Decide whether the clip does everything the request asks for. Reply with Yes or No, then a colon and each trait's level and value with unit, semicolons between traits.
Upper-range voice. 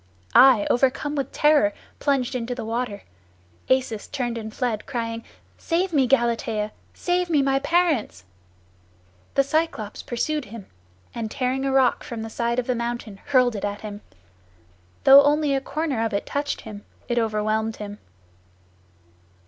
Yes: high, 245 Hz